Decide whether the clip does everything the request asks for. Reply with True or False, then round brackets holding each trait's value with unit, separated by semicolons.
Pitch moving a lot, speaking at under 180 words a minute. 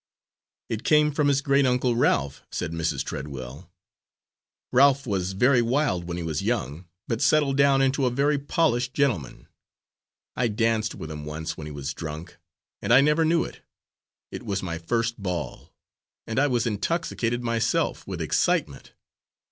True (8.3 semitones; 160 wpm)